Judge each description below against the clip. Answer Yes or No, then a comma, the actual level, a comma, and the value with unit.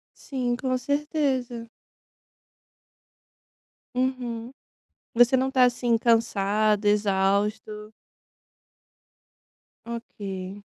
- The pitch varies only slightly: No, average, 3.3 semitones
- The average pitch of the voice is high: Yes, high, 230 Hz